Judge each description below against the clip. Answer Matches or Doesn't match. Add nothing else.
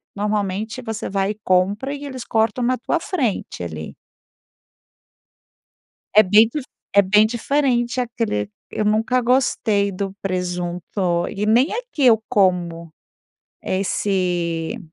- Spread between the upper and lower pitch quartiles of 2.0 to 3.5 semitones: Doesn't match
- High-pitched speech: Matches